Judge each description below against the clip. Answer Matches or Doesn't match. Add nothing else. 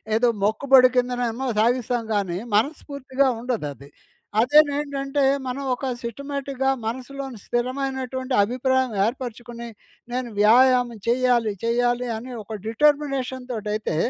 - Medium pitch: Doesn't match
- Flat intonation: Matches